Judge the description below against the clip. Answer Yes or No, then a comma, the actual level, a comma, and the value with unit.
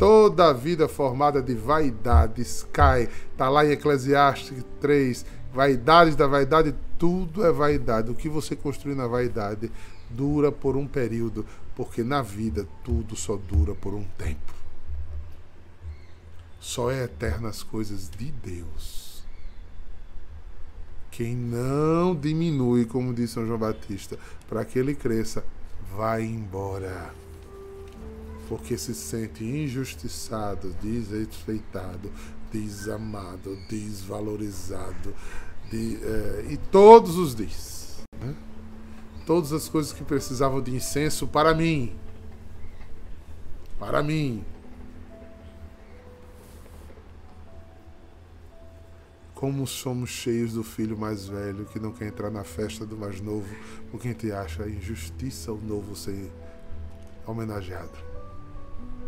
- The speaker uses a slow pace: Yes, slow, 110 wpm